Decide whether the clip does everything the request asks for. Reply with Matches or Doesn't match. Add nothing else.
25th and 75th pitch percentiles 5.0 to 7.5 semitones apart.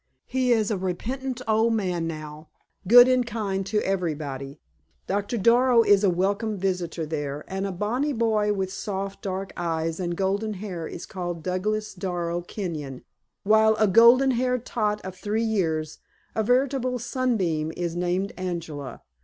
Doesn't match